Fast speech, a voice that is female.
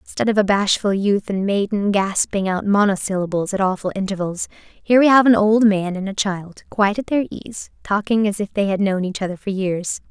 Yes: fast, 215 wpm; female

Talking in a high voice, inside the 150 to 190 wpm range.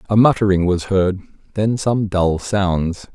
No: very low, 95 Hz; average, 155 wpm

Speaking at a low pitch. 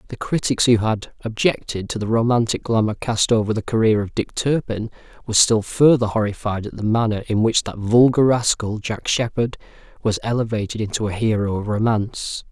Yes: low, 110 Hz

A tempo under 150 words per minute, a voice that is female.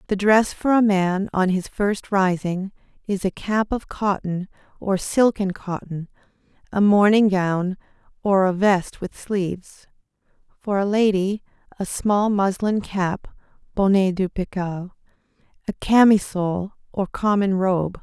Yes: slow, 135 wpm; female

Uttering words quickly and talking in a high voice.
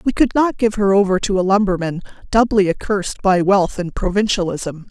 No: average, 185 wpm; high, 195 Hz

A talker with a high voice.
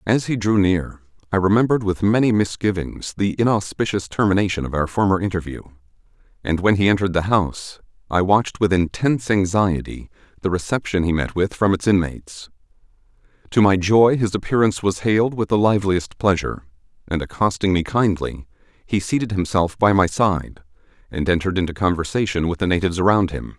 No: very low, 95 Hz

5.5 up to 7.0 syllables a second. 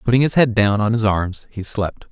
No: 5.2 syllables/s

